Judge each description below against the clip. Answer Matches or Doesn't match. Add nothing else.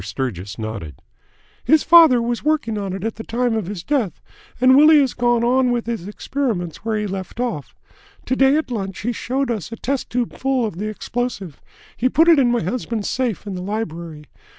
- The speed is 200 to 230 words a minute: Matches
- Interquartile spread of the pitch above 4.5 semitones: Matches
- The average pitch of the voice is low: Doesn't match